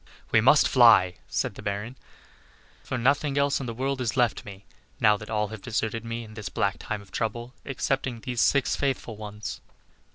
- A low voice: Yes, low, 115 Hz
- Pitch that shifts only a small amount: No, average, 3.4 semitones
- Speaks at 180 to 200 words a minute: Yes, average, 190 wpm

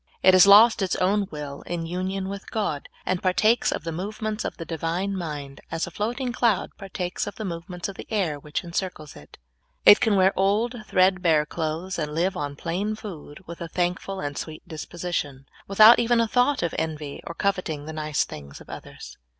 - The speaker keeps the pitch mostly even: No, average, 4.0 semitones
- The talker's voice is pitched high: No, medium, 180 Hz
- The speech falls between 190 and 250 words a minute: Yes, average, 200 wpm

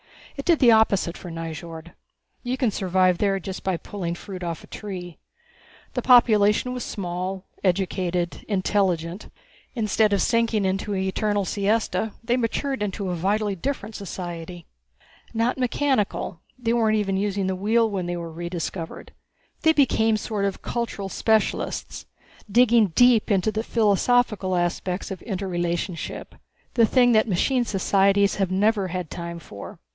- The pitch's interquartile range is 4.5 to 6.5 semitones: No, average, 3.7 semitones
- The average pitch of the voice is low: No, high, 200 Hz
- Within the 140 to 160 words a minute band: Yes, average, 145 wpm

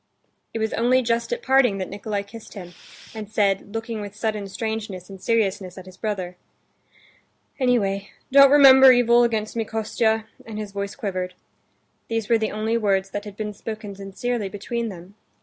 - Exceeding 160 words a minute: Yes, average, 170 wpm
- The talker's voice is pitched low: No, high, 215 Hz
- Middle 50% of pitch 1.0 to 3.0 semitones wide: Yes, average, 2.7 semitones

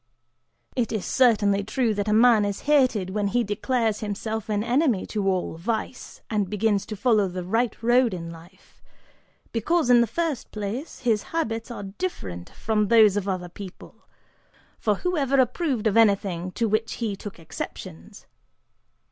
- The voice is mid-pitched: No, high, 215 Hz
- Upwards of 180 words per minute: No, average, 165 wpm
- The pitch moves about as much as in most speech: Yes, average, 3.3 semitones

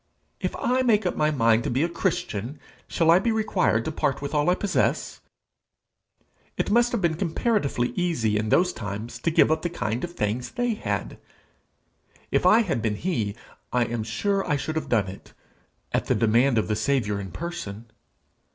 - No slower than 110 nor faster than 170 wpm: No, average, 190 wpm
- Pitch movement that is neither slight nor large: No, wide, 8.2 semitones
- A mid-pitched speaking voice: Yes, medium, 145 Hz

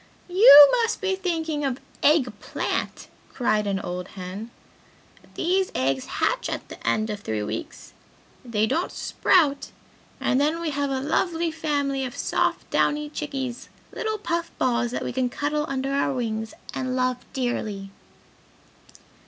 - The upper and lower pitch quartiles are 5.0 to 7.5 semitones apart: Yes, wide, 5.4 semitones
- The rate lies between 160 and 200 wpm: No, average, 145 wpm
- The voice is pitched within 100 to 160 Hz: No, very high, 270 Hz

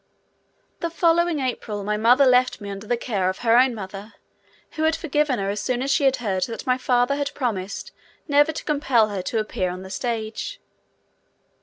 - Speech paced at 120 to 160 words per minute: No, average, 195 wpm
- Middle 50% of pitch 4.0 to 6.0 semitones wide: Yes, average, 5.2 semitones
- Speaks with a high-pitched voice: Yes, high, 245 Hz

